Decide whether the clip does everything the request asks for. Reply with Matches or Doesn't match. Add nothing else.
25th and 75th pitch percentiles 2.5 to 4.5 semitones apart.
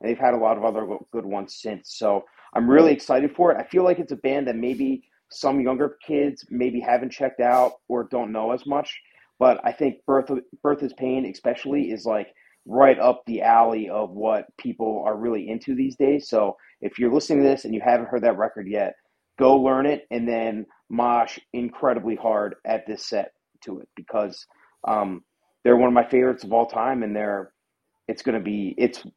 Matches